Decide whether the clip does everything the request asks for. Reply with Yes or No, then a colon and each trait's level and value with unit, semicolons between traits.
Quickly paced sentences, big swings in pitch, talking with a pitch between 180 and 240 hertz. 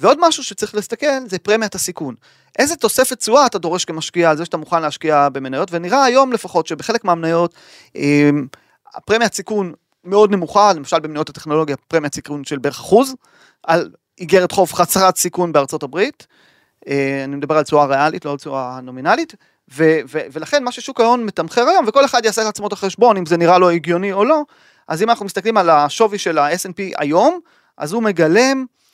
Yes: fast, 170 wpm; wide, 6.6 semitones; medium, 185 Hz